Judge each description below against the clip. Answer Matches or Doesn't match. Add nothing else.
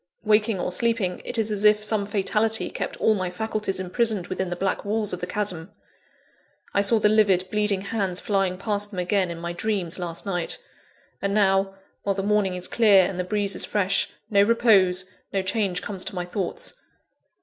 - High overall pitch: Matches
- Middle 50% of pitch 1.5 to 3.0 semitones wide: Matches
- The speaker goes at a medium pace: Matches